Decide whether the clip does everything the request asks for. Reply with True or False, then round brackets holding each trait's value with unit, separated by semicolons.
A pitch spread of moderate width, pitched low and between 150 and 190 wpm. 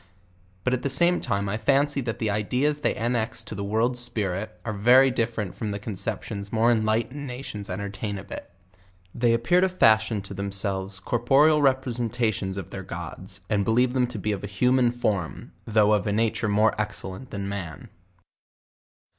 True (3.5 semitones; 110 Hz; 175 wpm)